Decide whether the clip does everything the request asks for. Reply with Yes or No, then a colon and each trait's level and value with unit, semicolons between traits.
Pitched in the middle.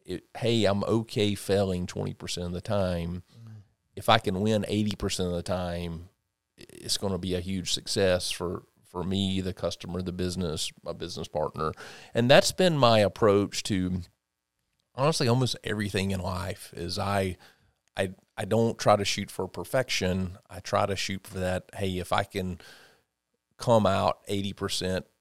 No: very low, 95 Hz